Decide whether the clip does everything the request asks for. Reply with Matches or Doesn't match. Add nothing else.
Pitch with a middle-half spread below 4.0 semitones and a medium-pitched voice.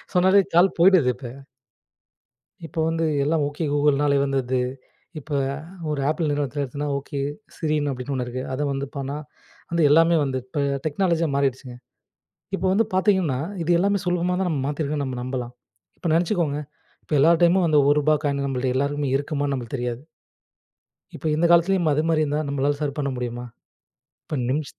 Matches